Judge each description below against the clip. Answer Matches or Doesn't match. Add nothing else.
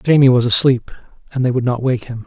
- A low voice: Matches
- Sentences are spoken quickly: Matches